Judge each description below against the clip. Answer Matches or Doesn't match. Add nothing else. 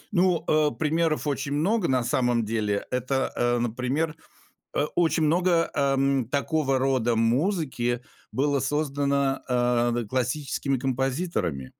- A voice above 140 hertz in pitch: Doesn't match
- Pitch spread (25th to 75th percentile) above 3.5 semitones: Matches